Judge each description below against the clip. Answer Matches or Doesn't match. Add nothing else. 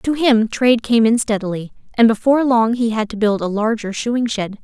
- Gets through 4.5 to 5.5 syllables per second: Matches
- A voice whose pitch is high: Matches